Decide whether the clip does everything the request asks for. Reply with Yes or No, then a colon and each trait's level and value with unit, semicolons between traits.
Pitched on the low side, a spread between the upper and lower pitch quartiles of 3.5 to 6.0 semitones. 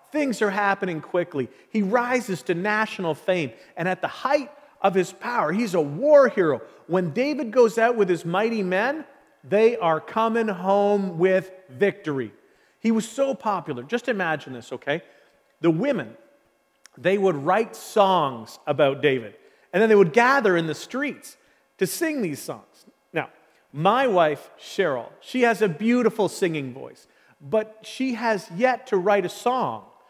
No: high, 205 Hz; average, 5.3 semitones